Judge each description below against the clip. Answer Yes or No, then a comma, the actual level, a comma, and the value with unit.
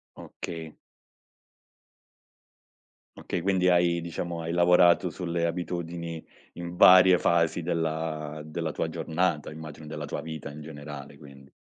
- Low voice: Yes, very low, 85 Hz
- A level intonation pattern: Yes, narrow, 2.0 semitones